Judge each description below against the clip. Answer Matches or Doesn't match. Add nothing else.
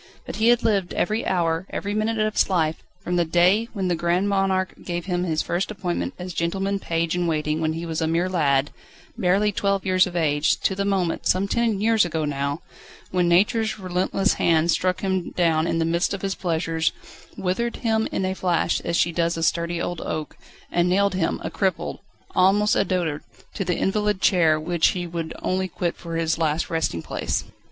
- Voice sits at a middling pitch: Matches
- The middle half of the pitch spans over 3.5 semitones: Doesn't match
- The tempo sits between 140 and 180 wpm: Doesn't match